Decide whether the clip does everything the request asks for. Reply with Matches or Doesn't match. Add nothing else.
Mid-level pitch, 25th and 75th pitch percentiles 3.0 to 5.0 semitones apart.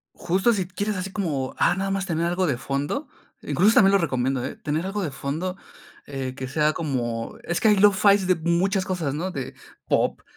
Doesn't match